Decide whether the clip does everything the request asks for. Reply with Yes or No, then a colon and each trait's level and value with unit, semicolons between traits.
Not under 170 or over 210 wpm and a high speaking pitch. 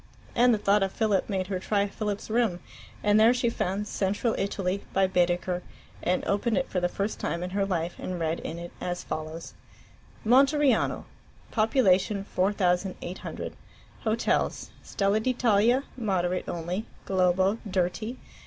No: average, 145 wpm; high, 195 Hz